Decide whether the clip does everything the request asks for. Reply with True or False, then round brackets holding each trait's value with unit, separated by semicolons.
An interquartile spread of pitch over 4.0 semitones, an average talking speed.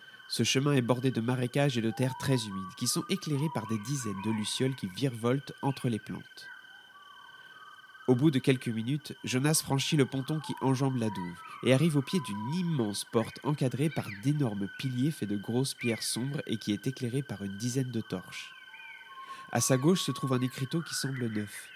True (4.8 semitones; 200 wpm)